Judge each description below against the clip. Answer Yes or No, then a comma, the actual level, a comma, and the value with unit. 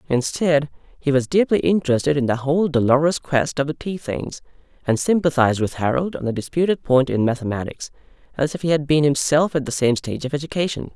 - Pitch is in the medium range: Yes, medium, 145 Hz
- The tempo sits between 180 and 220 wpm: Yes, average, 195 wpm